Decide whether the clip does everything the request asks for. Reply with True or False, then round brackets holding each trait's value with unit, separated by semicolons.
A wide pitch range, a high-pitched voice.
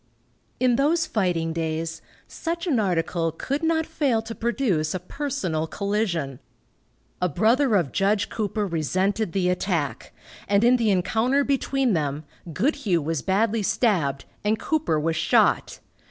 True (6.8 semitones; 200 Hz)